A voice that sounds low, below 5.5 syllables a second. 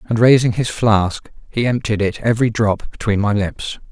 Yes: low, 110 Hz; 4.8 syllables/s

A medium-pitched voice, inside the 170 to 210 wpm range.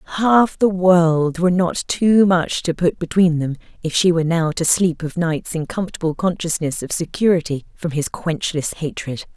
Yes: medium, 170 Hz; average, 180 wpm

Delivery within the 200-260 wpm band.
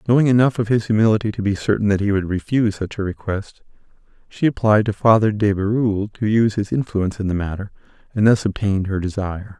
Yes: fast, 205 wpm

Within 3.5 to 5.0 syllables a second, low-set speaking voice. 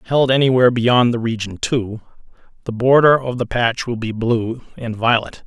Yes: 4.8 syllables/s; low, 120 Hz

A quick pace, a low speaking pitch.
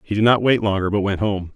Yes: fast, 310 wpm; low, 105 Hz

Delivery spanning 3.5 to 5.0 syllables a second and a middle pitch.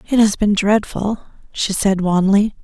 No: 4.2 syllables/s; high, 200 Hz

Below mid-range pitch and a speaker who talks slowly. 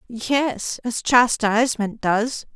No: high, 235 Hz; slow, 95 wpm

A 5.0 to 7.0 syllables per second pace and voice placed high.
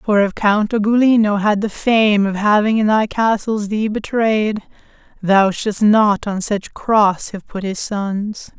No: 3.8 syllables/s; high, 210 Hz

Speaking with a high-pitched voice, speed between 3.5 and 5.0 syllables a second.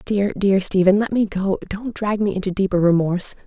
No: high, 195 Hz; 5.5 syllables/s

